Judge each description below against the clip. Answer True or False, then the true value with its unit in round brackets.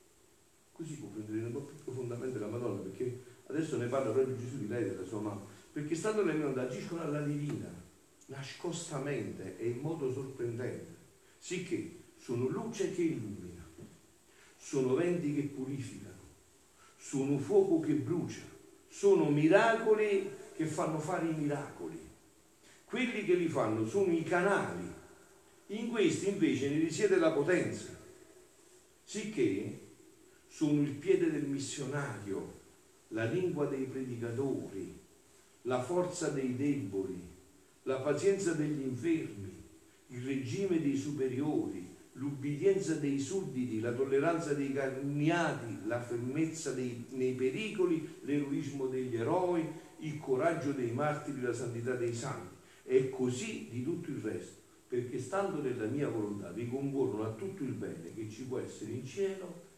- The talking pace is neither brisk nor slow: True (135 wpm)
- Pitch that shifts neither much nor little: False (6.0 semitones)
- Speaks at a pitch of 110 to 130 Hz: False (140 Hz)